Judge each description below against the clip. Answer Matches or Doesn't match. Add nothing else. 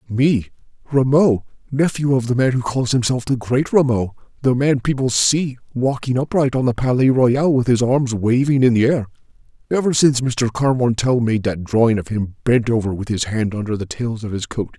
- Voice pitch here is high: Doesn't match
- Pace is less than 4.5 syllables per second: Doesn't match